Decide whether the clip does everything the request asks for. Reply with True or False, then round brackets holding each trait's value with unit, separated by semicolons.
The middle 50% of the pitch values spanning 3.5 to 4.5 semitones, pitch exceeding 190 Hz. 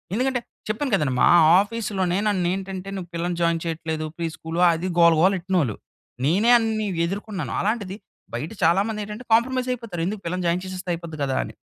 False (4.0 semitones; 185 Hz)